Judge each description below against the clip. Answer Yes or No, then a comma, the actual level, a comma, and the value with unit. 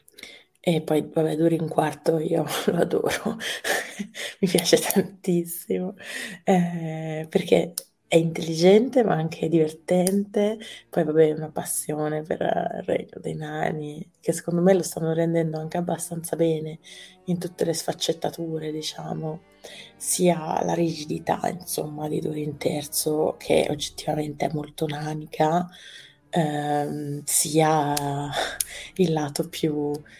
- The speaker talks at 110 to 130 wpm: Yes, average, 120 wpm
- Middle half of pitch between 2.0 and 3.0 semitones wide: Yes, narrow, 2.6 semitones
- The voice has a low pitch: No, medium, 160 Hz